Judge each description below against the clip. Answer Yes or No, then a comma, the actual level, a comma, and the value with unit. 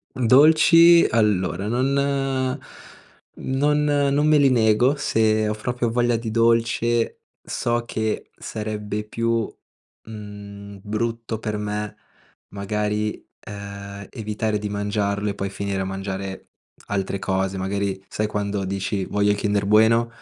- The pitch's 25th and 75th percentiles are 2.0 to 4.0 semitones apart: Yes, narrow, 2.5 semitones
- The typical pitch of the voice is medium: No, low, 105 Hz